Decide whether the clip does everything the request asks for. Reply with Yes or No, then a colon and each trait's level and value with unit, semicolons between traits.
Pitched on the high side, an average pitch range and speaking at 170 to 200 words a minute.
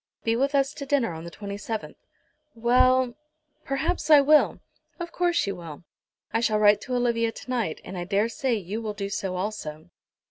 Yes: high, 225 Hz; average, 5.0 semitones; average, 180 wpm